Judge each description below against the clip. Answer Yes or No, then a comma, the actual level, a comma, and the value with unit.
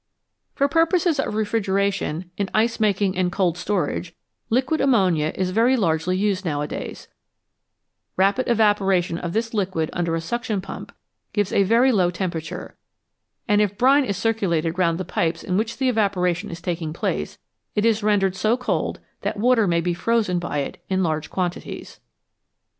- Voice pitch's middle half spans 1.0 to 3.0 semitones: No, average, 4.3 semitones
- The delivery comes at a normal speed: Yes, average, 160 wpm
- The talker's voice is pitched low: No, high, 195 Hz